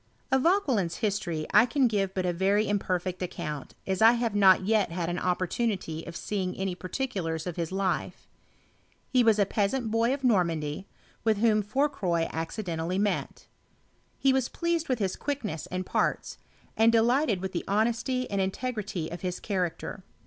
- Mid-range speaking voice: No, high, 200 Hz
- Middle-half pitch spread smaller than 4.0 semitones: No, average, 4.3 semitones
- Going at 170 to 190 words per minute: Yes, average, 180 wpm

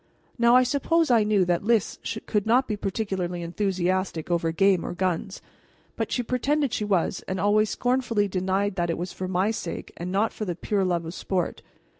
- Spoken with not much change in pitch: No, average, 3.7 semitones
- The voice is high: Yes, high, 195 Hz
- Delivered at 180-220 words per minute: Yes, average, 195 wpm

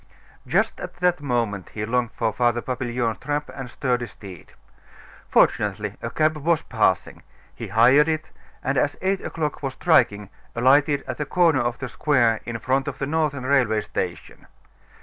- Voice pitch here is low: Yes, low, 130 Hz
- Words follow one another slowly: No, average, 165 wpm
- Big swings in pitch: No, average, 4.1 semitones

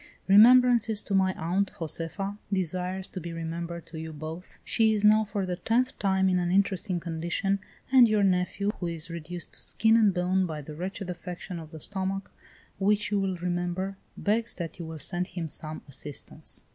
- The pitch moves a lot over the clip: No, average, 2.8 semitones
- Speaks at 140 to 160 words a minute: No, average, 185 wpm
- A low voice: No, medium, 185 Hz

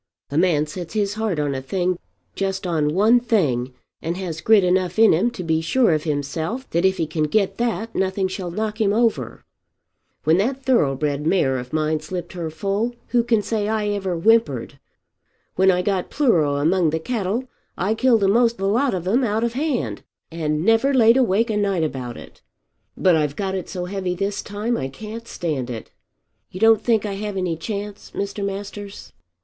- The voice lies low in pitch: No, high, 190 Hz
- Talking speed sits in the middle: Yes, average, 195 wpm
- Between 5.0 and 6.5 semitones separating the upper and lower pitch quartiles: Yes, average, 5.3 semitones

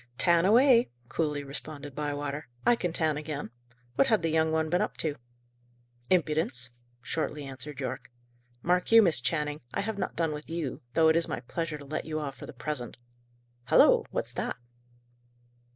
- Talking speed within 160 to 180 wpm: Yes, average, 175 wpm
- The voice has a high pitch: No, medium, 155 Hz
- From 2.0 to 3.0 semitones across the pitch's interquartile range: Yes, narrow, 2.6 semitones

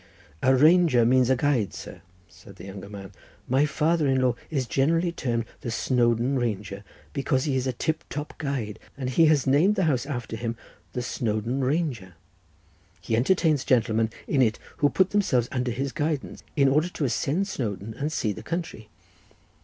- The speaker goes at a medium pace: Yes, average, 175 wpm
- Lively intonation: No, average, 4.6 semitones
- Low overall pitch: Yes, low, 130 Hz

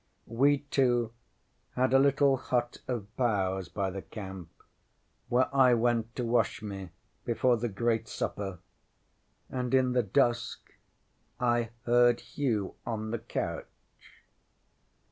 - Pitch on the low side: Yes, low, 120 Hz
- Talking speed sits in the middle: No, slow, 125 wpm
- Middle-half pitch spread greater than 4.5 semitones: No, average, 2.8 semitones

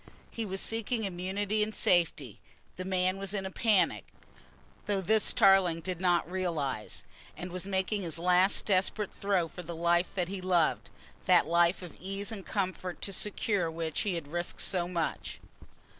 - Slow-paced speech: No, average, 170 wpm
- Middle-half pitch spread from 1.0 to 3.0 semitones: Yes, narrow, 2.4 semitones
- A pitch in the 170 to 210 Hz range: Yes, medium, 185 Hz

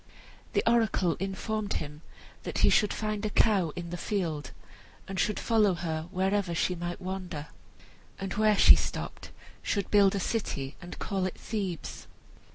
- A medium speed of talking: Yes, average, 160 wpm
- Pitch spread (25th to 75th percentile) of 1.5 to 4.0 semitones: Yes, average, 3.3 semitones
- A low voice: No, high, 190 Hz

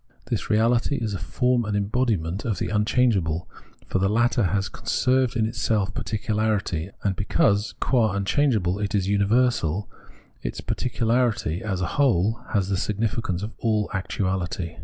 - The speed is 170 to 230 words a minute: No, average, 155 wpm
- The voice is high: No, low, 105 Hz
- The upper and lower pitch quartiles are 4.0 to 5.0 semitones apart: No, average, 3.3 semitones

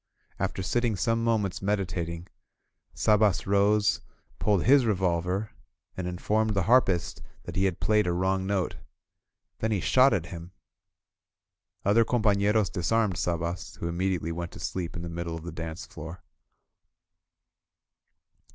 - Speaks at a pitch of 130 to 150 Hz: No, very low, 95 Hz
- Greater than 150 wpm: No, average, 140 wpm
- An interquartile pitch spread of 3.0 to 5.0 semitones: Yes, average, 3.7 semitones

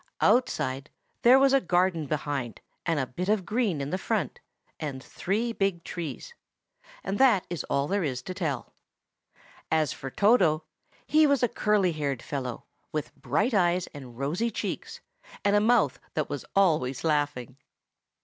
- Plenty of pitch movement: Yes, wide, 6.6 semitones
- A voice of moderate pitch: Yes, medium, 170 Hz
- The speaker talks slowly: No, average, 155 wpm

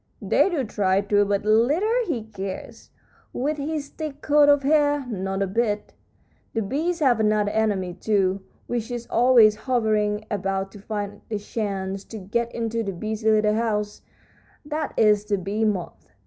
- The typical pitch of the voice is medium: No, high, 215 Hz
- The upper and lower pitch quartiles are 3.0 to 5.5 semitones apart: Yes, average, 3.7 semitones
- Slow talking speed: No, average, 160 wpm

